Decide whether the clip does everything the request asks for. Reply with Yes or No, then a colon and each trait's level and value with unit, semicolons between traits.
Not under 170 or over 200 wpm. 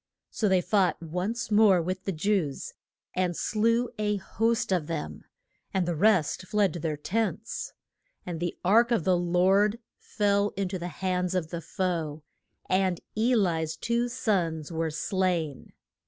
No: average, 155 wpm